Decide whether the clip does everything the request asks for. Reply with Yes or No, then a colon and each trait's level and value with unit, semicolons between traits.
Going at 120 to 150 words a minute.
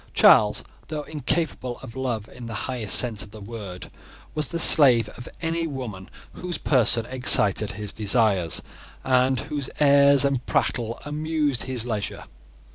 Yes: average, 145 wpm